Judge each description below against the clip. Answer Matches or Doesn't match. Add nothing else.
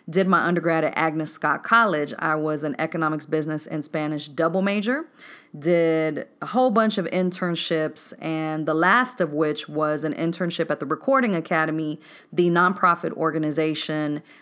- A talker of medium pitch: Matches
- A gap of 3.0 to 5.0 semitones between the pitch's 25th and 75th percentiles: Doesn't match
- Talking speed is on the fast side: Doesn't match